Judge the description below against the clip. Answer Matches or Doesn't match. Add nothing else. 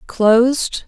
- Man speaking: Doesn't match